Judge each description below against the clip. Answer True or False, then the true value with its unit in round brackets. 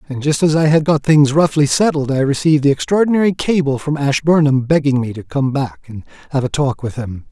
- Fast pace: True (220 wpm)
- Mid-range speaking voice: True (145 Hz)